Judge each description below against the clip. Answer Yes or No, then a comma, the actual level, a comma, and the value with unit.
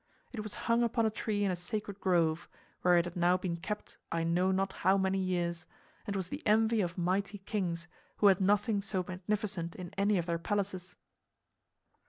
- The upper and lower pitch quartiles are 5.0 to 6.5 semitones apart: No, average, 2.8 semitones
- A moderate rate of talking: Yes, average, 195 wpm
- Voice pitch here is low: No, high, 190 Hz